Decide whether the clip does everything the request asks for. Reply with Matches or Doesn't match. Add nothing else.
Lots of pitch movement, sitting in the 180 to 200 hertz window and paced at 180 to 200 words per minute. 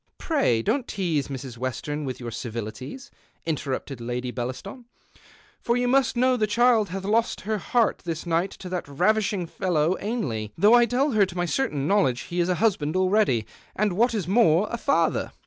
Matches